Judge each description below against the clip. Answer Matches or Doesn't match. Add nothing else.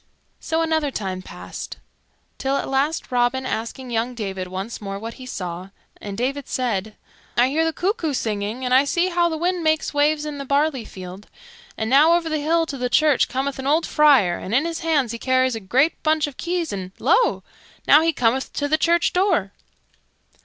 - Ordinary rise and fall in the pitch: Doesn't match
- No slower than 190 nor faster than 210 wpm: Matches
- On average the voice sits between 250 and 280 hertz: Matches